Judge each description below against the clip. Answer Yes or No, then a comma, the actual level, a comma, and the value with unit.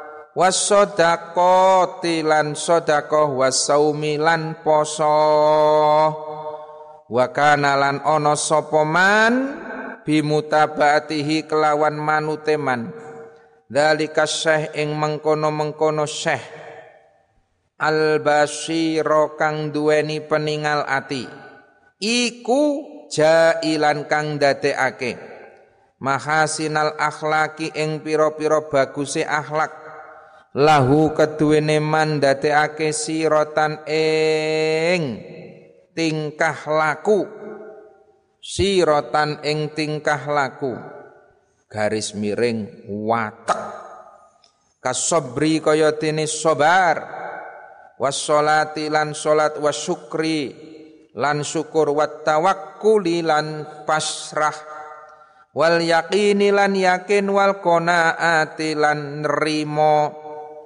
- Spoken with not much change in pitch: Yes, narrow, 0.8 semitones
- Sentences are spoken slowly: Yes, slow, 65 wpm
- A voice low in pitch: No, medium, 155 Hz